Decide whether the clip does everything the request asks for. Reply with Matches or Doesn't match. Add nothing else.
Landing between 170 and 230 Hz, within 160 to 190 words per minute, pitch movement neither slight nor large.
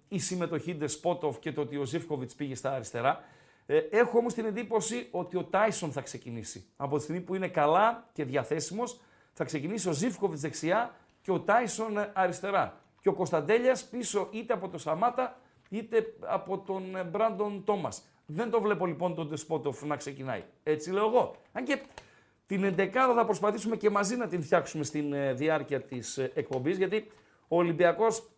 Doesn't match